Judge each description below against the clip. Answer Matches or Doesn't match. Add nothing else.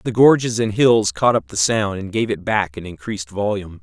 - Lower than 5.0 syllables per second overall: Doesn't match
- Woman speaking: Doesn't match